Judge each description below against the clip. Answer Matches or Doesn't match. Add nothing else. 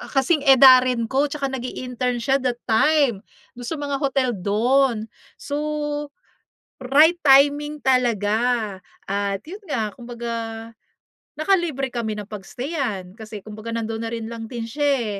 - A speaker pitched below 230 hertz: Doesn't match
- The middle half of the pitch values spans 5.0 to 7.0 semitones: Doesn't match